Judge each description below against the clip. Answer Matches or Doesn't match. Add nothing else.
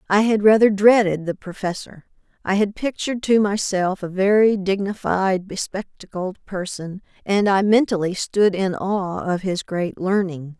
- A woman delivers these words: Matches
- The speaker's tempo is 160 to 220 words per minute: Doesn't match